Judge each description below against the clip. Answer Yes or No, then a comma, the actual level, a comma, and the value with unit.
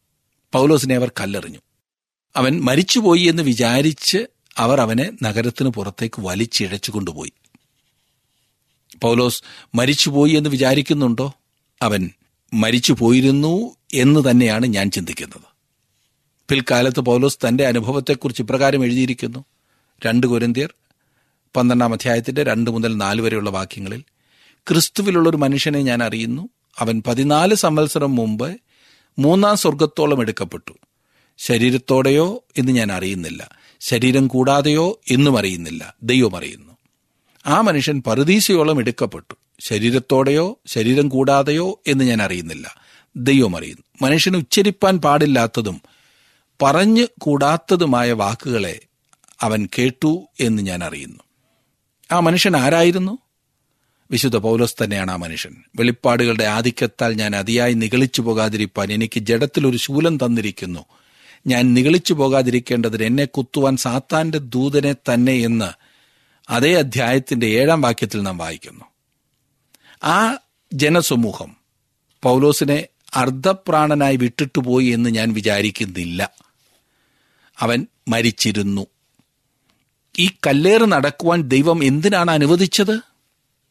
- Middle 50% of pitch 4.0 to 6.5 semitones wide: Yes, average, 4.3 semitones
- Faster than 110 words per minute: No, average, 95 wpm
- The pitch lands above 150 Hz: No, low, 130 Hz